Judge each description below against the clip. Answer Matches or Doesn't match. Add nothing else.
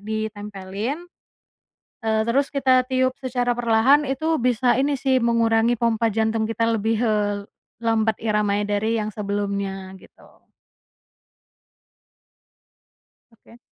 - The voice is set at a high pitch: Matches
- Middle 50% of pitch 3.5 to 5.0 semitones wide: Doesn't match